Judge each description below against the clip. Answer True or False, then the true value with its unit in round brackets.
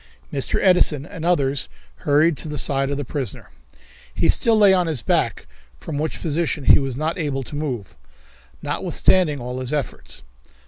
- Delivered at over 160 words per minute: True (170 wpm)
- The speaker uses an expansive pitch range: False (3.4 semitones)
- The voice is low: False (145 Hz)